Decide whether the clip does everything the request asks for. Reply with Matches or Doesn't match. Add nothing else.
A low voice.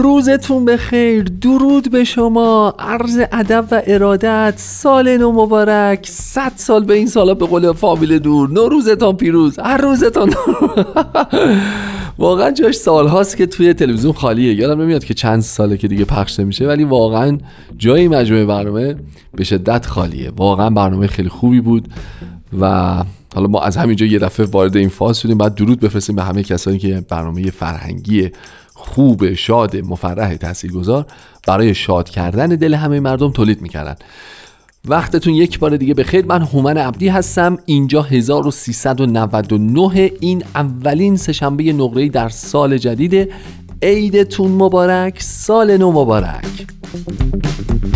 Doesn't match